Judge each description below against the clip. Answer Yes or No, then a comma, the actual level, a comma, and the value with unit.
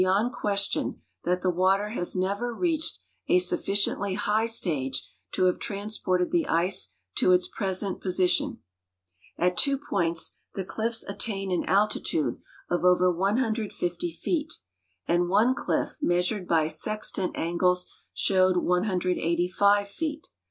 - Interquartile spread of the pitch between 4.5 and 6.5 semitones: No, average, 2.9 semitones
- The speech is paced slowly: Yes, slow, 125 wpm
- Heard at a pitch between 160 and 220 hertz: Yes, medium, 185 Hz